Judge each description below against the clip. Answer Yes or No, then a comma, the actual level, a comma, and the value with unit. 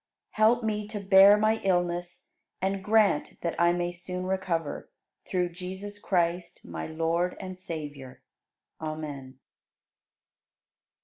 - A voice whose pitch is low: No, medium, 180 Hz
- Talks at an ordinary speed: No, slow, 115 wpm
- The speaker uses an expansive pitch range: No, average, 3.0 semitones